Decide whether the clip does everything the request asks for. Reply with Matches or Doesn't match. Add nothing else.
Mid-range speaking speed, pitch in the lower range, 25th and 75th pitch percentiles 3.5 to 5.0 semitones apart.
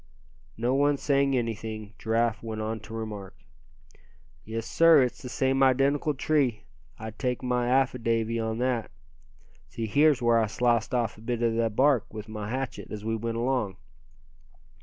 Doesn't match